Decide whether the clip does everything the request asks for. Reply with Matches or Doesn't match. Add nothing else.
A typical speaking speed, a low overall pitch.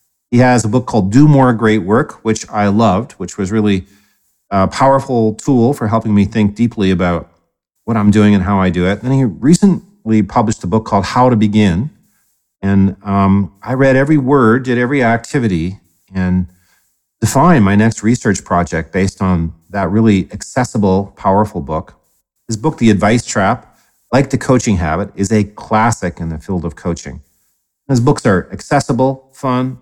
Matches